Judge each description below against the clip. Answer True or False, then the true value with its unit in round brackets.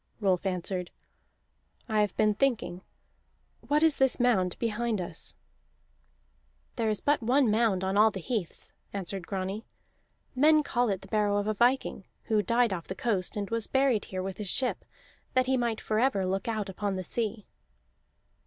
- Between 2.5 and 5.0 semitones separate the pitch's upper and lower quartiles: True (3.9 semitones)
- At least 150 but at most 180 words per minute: True (170 wpm)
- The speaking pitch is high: True (215 Hz)